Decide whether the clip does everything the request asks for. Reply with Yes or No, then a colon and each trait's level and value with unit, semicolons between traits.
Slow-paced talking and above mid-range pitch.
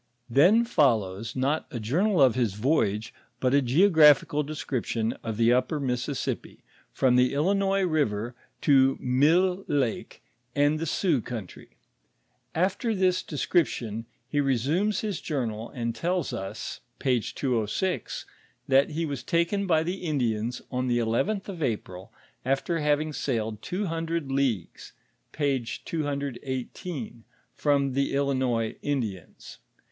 No: slow, 130 wpm; medium, 140 Hz